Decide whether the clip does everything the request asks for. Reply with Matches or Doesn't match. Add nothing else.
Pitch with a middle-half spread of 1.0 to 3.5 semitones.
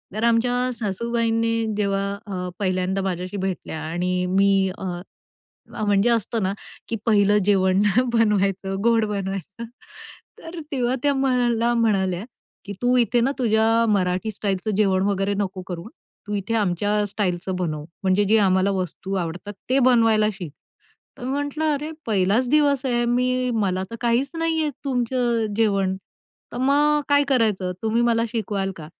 Doesn't match